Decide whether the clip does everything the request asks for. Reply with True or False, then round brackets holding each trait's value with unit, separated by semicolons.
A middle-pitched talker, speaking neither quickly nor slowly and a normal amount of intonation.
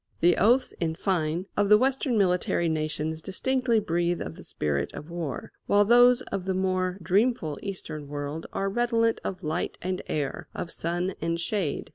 True (180 Hz; 170 wpm; 4.6 semitones)